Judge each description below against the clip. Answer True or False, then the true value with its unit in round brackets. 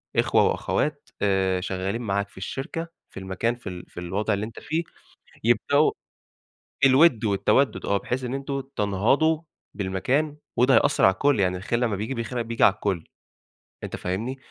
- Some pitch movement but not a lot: False (5.7 semitones)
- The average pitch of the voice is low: True (110 Hz)